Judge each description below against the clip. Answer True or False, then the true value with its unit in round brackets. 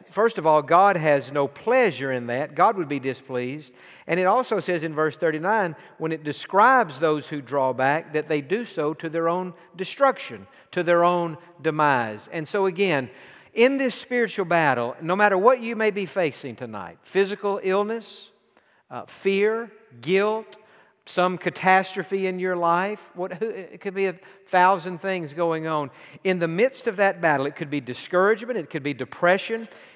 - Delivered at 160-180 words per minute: True (175 wpm)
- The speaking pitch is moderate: True (180 Hz)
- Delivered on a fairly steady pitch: False (4.7 semitones)